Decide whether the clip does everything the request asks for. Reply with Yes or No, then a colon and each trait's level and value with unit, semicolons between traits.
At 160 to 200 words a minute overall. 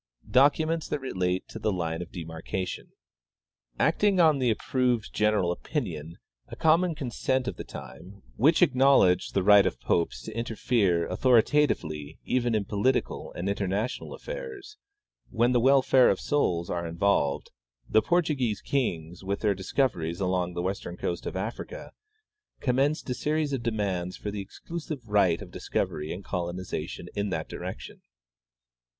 No: average, 150 wpm